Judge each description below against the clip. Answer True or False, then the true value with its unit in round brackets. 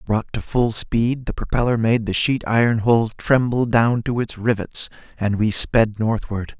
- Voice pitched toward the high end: False (115 Hz)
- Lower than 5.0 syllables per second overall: True (4.2 syllables/s)